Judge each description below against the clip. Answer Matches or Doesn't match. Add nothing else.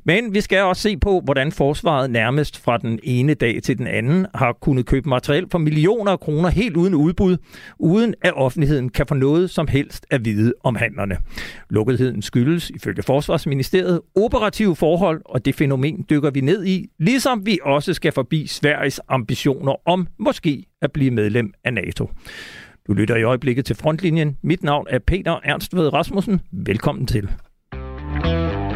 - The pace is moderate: Matches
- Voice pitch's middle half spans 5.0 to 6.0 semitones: Matches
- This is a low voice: Doesn't match